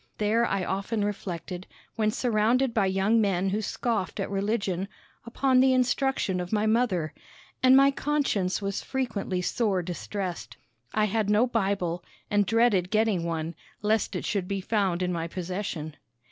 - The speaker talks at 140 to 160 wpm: Yes, average, 155 wpm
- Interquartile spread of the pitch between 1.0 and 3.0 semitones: No, average, 3.7 semitones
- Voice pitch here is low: No, high, 200 Hz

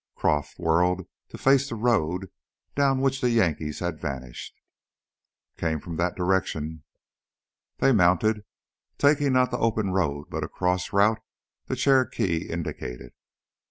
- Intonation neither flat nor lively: No, wide, 6.7 semitones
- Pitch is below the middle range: Yes, very low, 95 Hz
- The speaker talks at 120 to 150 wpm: Yes, slow, 135 wpm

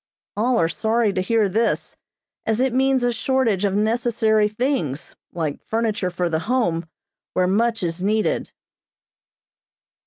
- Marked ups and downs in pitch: No, average, 4.4 semitones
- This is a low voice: No, high, 220 Hz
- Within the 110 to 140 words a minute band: Yes, slow, 135 wpm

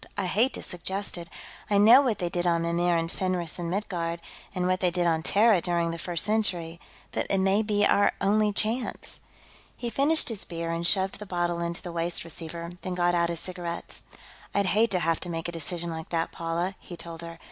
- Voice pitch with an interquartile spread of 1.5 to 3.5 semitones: Yes, average, 2.9 semitones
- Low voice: No, medium, 175 Hz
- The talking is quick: Yes, fast, 220 wpm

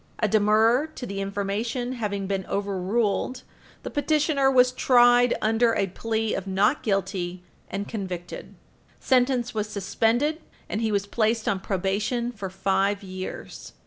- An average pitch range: Yes, average, 3.7 semitones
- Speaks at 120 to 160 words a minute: Yes, average, 140 wpm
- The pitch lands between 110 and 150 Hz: No, high, 215 Hz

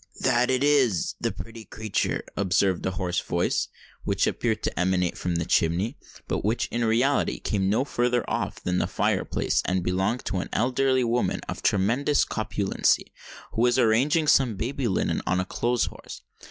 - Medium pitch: No, low, 110 Hz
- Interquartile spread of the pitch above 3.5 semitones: Yes, average, 4.8 semitones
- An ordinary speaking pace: Yes, average, 175 wpm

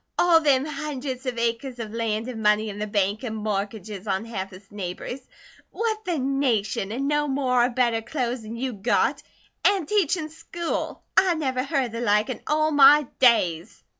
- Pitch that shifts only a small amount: No, average, 5.0 semitones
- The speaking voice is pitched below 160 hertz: No, high, 245 Hz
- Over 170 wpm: Yes, average, 185 wpm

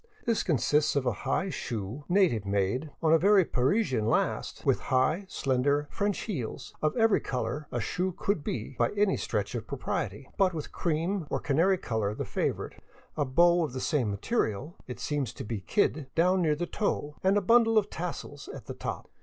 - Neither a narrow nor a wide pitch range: No, wide, 6.7 semitones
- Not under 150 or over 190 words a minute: No, average, 200 wpm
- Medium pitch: Yes, medium, 150 Hz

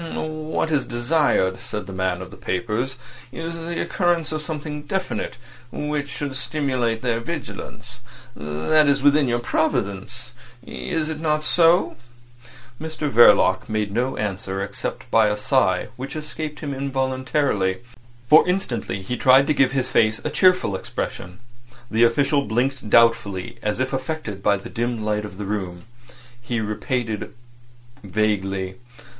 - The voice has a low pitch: Yes, low, 125 Hz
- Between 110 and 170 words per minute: Yes, average, 140 wpm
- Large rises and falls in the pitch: Yes, wide, 6.1 semitones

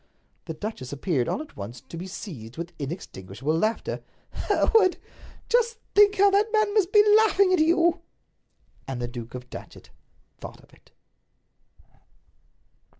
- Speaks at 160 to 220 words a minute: No, average, 150 wpm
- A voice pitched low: No, high, 210 Hz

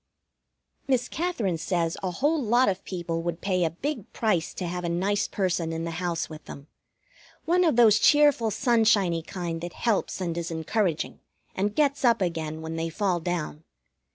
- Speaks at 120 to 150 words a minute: No, average, 180 wpm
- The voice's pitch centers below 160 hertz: No, medium, 180 Hz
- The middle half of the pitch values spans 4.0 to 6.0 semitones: Yes, wide, 5.4 semitones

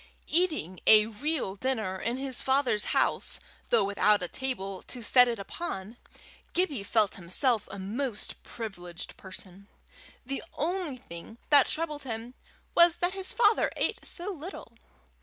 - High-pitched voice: Yes, high, 240 Hz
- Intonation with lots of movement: Yes, wide, 6.9 semitones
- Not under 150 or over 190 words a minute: No, average, 140 wpm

